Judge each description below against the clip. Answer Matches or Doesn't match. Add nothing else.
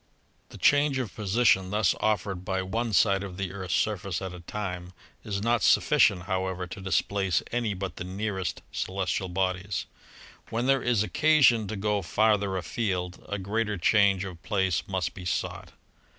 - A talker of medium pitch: Doesn't match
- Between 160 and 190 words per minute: Matches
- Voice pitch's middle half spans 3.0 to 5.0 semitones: Doesn't match